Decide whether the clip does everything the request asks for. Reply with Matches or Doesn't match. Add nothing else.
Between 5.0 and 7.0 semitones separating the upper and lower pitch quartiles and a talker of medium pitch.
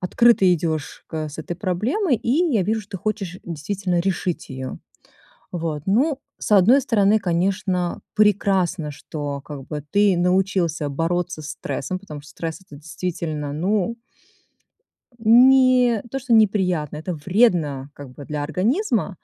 Matches